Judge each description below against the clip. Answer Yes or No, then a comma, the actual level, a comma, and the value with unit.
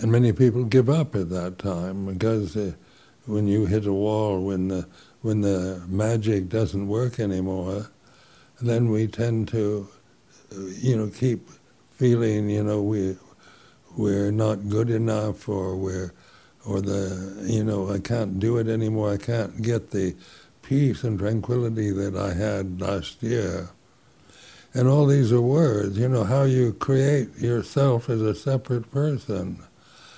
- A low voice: Yes, low, 110 Hz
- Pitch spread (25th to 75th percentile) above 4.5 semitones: No, average, 3.3 semitones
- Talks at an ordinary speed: Yes, average, 150 wpm